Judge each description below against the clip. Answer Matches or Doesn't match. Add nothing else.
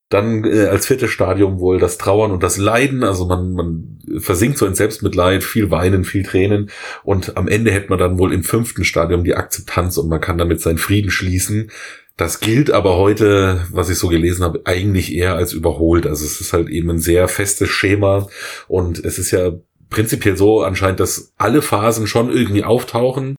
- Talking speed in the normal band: Doesn't match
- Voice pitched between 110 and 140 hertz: Doesn't match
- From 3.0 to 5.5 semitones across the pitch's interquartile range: Doesn't match